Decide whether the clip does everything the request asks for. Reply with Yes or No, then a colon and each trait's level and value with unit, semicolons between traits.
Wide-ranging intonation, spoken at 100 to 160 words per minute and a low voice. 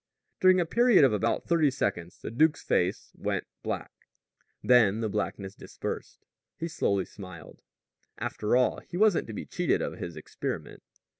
Yes: wide, 8.6 semitones; average, 155 wpm; low, 115 Hz